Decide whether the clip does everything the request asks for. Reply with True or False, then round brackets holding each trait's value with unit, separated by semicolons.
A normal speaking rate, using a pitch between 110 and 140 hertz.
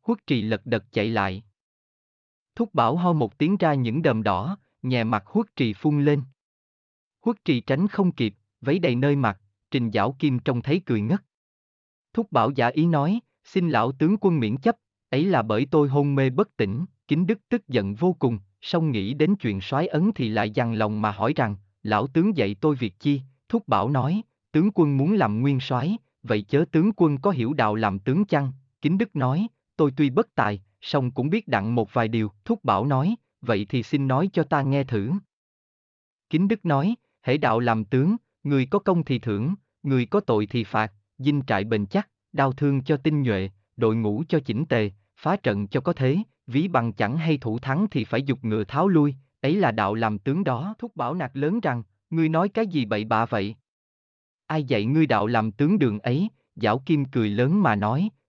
True (210 wpm; 135 Hz)